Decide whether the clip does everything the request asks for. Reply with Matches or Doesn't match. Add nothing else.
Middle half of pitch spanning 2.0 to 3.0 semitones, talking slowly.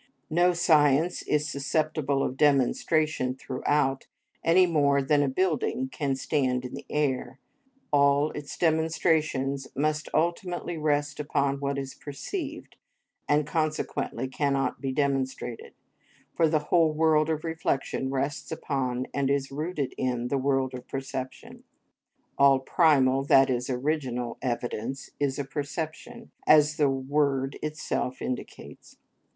Matches